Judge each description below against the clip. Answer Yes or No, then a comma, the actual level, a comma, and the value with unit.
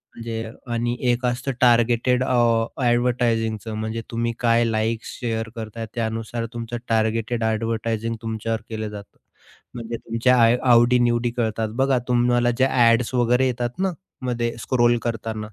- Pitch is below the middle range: Yes, low, 115 Hz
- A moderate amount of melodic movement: No, narrow, 1.3 semitones